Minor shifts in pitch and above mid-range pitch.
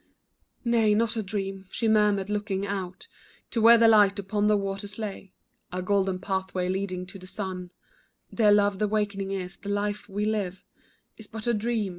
Yes: narrow, 1.8 semitones; high, 205 Hz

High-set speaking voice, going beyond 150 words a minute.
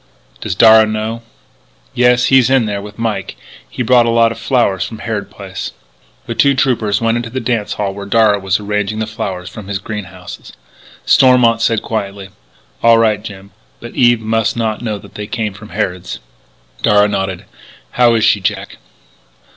No: low, 110 Hz; average, 175 wpm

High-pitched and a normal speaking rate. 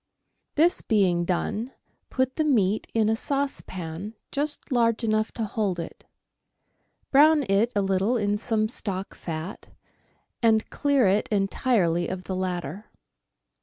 No: high, 215 Hz; slow, 130 wpm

